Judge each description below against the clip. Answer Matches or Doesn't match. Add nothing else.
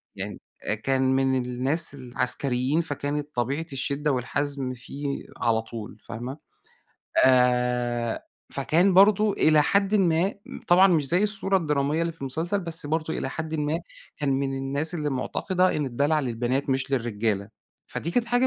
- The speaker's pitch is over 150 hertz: Doesn't match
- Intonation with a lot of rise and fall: Doesn't match